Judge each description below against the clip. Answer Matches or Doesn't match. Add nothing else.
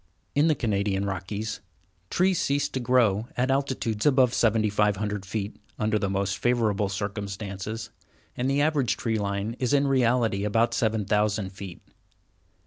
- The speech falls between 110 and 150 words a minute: Matches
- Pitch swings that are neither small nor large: Matches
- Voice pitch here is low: Matches